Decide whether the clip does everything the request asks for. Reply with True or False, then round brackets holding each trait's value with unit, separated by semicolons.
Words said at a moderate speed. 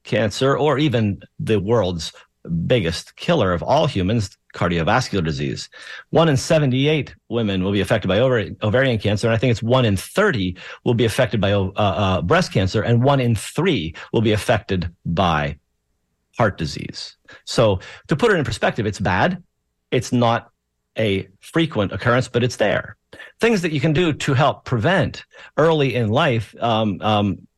True (165 wpm)